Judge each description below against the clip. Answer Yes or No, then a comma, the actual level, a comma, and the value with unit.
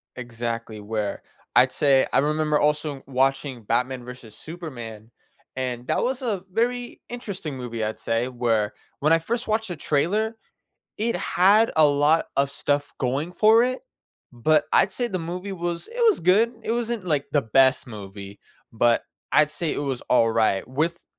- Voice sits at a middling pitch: Yes, medium, 145 Hz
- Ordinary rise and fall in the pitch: No, wide, 7.3 semitones